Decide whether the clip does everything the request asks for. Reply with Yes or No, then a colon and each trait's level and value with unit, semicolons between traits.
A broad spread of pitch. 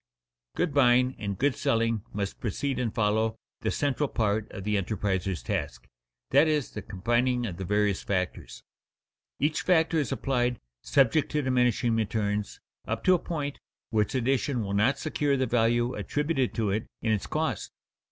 No: average, 4.7 semitones